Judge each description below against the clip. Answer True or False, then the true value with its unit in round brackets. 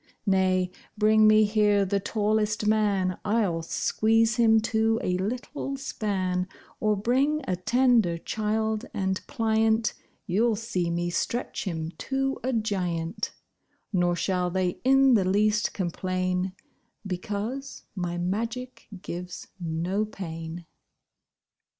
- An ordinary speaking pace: False (115 wpm)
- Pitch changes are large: False (3.5 semitones)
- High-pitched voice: True (210 Hz)